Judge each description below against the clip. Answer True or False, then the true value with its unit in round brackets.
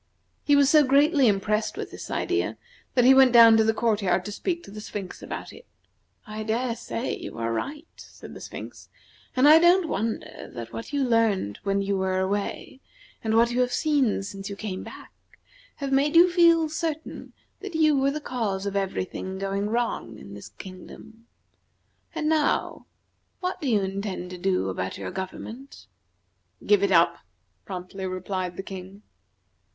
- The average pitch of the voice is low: False (220 Hz)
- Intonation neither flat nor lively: False (6.3 semitones)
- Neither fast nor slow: True (180 wpm)